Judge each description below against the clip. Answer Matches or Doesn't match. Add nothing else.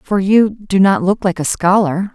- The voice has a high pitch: Matches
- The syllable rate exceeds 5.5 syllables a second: Doesn't match